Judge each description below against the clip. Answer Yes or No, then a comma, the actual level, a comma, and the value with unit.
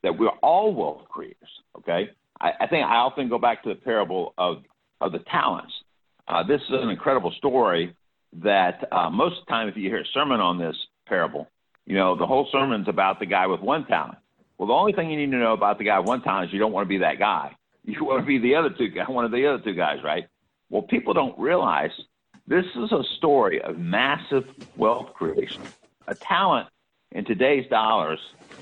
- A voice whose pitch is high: No, low, 130 Hz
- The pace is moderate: No, fast, 220 wpm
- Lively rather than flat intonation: Yes, wide, 6.9 semitones